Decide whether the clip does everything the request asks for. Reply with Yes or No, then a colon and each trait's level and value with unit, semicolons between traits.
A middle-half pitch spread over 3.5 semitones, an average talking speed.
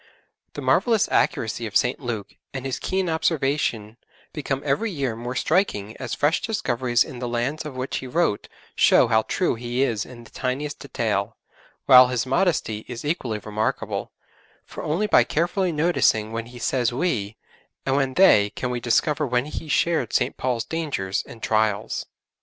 Yes: average, 4.9 semitones; average, 170 wpm